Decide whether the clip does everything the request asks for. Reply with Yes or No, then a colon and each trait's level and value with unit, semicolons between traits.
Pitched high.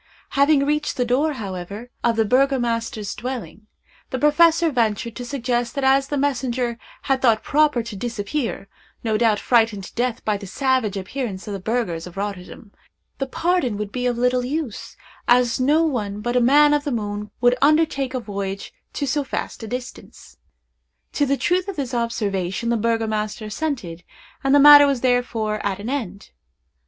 Yes: high, 245 Hz